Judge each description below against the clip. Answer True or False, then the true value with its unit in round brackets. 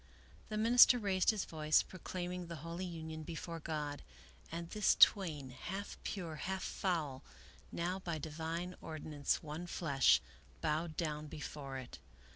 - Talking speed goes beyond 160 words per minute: False (135 wpm)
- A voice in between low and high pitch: True (165 Hz)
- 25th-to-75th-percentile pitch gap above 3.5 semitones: False (3.1 semitones)